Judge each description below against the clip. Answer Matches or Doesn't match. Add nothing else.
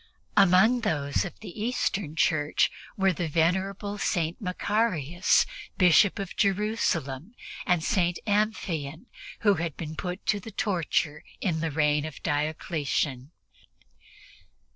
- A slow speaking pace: Matches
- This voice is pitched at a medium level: Matches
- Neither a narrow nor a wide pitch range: Matches